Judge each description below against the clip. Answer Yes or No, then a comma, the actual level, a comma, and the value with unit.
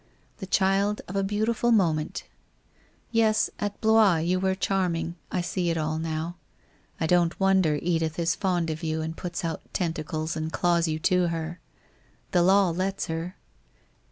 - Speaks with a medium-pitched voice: Yes, medium, 175 Hz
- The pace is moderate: Yes, average, 160 wpm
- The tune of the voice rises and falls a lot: No, average, 3.0 semitones